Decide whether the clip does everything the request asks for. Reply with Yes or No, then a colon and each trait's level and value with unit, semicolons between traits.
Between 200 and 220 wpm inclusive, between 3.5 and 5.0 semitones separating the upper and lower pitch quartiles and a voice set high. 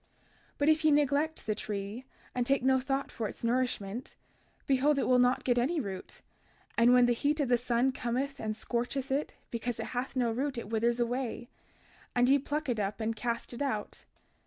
No: fast, 205 wpm; average, 2.8 semitones; high, 245 Hz